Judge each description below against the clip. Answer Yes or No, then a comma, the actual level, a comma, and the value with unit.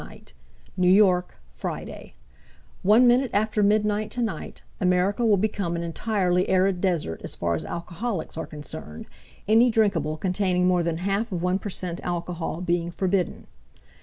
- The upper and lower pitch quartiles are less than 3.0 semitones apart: No, average, 3.3 semitones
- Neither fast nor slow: Yes, average, 145 wpm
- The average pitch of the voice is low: No, medium, 185 Hz